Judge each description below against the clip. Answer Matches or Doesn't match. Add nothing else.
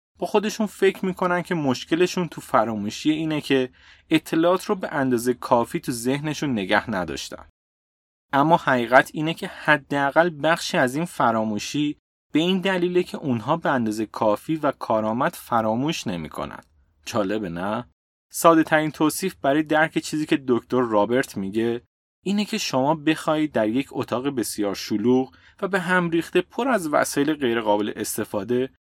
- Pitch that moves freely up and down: Matches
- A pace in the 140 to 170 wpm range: Matches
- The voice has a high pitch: Doesn't match